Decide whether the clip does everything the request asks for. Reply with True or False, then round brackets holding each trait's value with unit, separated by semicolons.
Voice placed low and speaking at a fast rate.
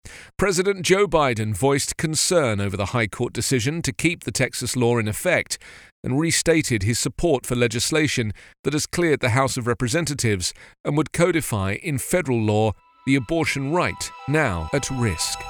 False (130 Hz; 165 wpm)